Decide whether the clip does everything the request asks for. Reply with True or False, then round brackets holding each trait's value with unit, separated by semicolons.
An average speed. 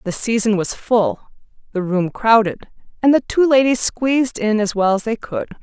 True (190 wpm)